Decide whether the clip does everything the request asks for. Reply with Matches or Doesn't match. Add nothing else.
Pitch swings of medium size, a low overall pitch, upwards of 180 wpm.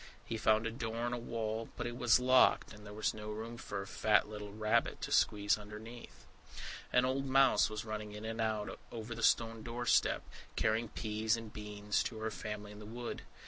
Doesn't match